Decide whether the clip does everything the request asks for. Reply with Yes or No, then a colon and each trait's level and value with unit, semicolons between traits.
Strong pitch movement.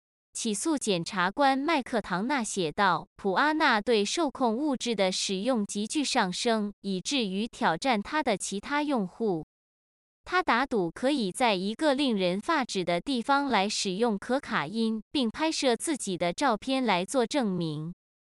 Yes: wide, 5.8 semitones